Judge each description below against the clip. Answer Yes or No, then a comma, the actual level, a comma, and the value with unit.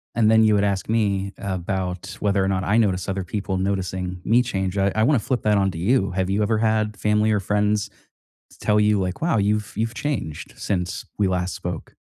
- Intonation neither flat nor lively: No, narrow, 2.2 semitones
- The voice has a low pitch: Yes, low, 100 Hz